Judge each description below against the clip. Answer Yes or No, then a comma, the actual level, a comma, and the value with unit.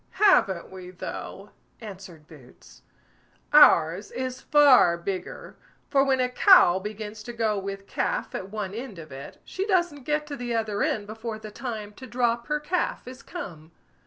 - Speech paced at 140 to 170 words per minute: Yes, average, 165 wpm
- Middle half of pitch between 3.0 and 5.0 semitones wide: No, wide, 5.5 semitones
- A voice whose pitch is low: No, high, 220 Hz